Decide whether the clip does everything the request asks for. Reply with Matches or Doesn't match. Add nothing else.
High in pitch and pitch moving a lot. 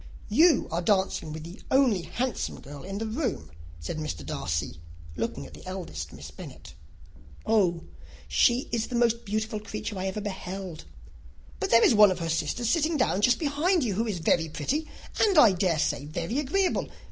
Matches